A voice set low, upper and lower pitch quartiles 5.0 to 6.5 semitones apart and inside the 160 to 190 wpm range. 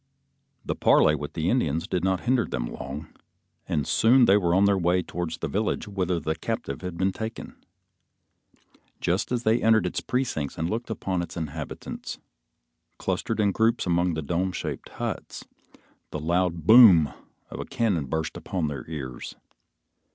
Yes: very low, 90 Hz; average, 5.3 semitones; average, 165 wpm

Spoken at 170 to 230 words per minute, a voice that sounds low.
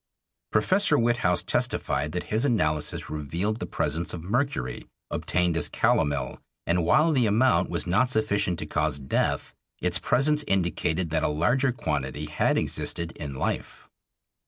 No: average, 145 wpm; very low, 90 Hz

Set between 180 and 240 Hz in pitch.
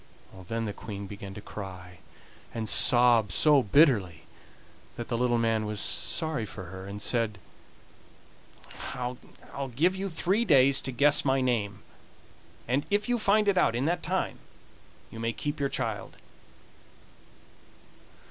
No: low, 120 Hz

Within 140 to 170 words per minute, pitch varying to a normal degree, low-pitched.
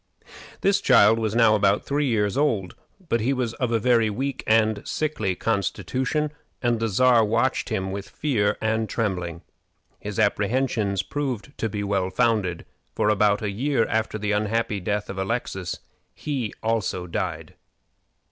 Yes: average, 155 wpm; average, 3.1 semitones; low, 110 Hz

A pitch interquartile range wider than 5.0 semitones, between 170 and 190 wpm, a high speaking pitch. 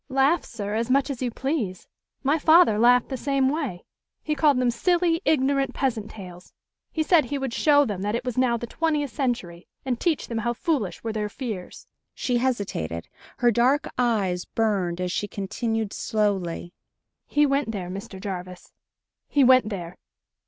Yes: wide, 5.4 semitones; average, 175 wpm; high, 240 Hz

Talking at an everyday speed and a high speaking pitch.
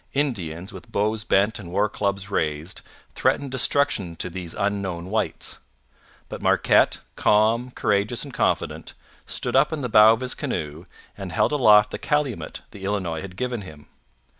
No: average, 160 wpm; low, 100 Hz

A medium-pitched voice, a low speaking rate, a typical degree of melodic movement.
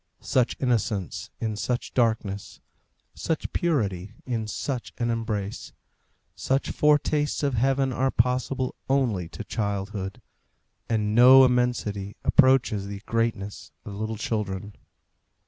No: low, 115 Hz; slow, 110 wpm; average, 4.0 semitones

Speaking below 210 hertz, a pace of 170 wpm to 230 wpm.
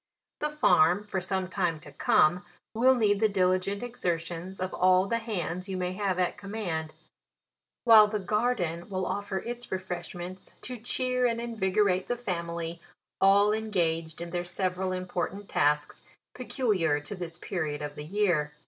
No: medium, 185 Hz; average, 155 wpm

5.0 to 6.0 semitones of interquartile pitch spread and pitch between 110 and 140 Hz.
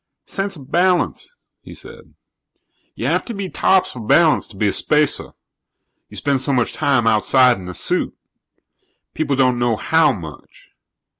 Yes: wide, 5.6 semitones; low, 135 Hz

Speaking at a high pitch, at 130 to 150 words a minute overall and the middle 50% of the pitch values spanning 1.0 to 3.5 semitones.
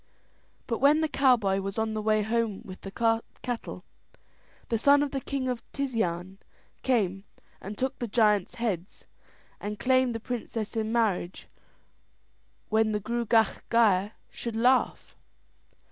Yes: high, 225 Hz; average, 140 wpm; average, 3.1 semitones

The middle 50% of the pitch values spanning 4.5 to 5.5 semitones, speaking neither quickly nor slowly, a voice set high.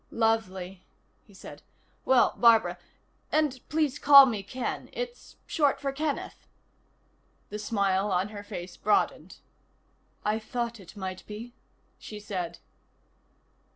No: average, 5.0 semitones; slow, 120 wpm; high, 215 Hz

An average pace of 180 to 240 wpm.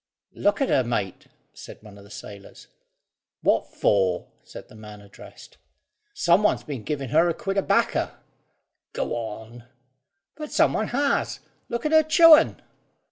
No: average, 155 wpm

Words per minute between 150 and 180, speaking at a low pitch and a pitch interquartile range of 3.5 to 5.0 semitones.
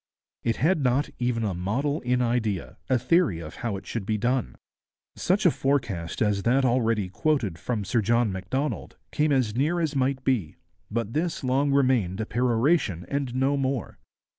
Yes: average, 175 wpm; low, 125 Hz; average, 4.5 semitones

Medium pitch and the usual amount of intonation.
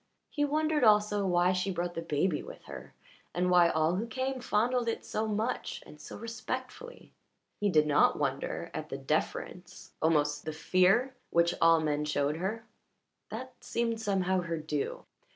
No: medium, 180 Hz; wide, 6.1 semitones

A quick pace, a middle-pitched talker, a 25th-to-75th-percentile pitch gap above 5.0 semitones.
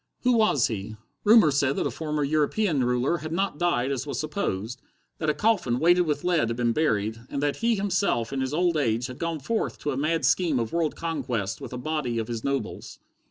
Yes: fast, 220 wpm; medium, 145 Hz; wide, 5.5 semitones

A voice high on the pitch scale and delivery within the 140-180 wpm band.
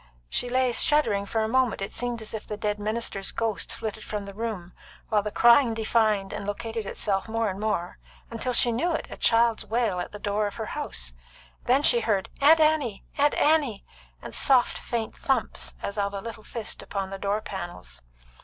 No: high, 220 Hz; average, 195 wpm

